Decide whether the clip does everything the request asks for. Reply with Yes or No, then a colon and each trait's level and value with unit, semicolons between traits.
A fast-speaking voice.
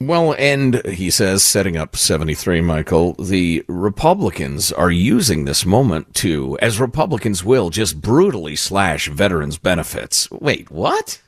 No: slow, 135 wpm